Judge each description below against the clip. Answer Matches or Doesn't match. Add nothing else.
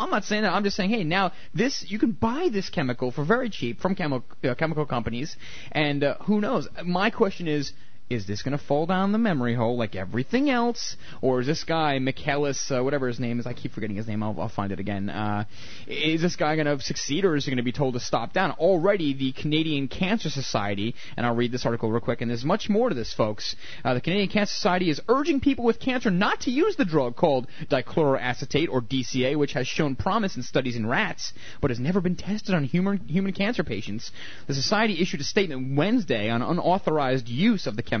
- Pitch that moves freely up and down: Matches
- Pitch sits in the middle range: Matches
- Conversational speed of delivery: Doesn't match